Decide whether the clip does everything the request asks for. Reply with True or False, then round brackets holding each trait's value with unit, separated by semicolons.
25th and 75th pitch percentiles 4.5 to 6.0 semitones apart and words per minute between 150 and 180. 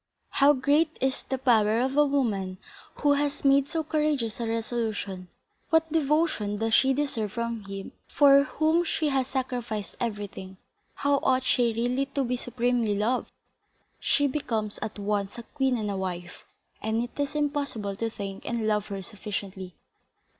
True (5.1 semitones; 160 wpm)